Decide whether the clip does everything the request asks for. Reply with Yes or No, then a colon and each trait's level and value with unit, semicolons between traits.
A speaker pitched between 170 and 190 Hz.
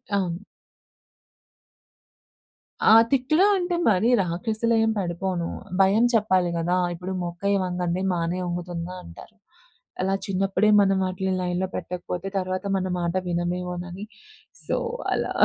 Yes: medium, 185 Hz